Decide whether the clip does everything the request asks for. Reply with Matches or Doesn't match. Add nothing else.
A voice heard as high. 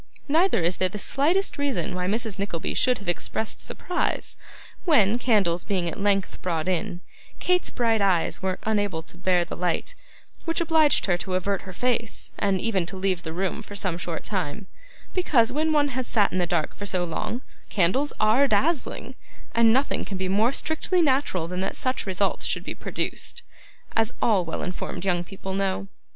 Matches